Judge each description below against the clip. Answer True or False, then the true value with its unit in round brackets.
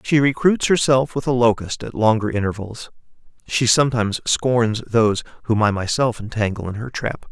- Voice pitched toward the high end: False (115 Hz)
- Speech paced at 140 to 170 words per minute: True (165 wpm)